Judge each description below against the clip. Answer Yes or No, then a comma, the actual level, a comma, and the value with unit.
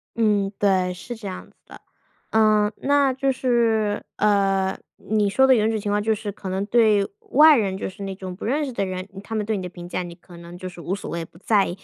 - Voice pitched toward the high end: Yes, high, 205 Hz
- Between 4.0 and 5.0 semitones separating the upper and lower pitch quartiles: No, average, 2.9 semitones